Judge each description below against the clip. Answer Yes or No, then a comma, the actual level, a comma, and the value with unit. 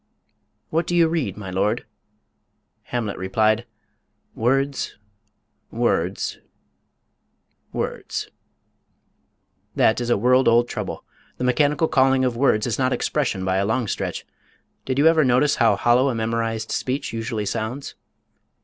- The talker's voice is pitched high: No, low, 120 Hz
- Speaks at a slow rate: Yes, slow, 130 wpm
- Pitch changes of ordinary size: Yes, average, 3.4 semitones